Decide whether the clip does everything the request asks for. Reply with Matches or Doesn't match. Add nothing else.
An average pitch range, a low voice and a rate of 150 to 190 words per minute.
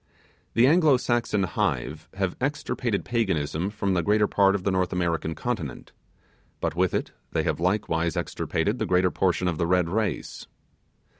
Matches